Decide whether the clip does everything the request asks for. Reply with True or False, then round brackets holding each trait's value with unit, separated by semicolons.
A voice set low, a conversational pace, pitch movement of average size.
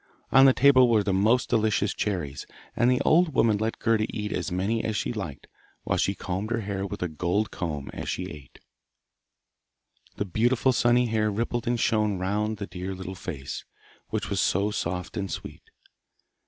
True (105 Hz; 180 wpm; 3.7 semitones)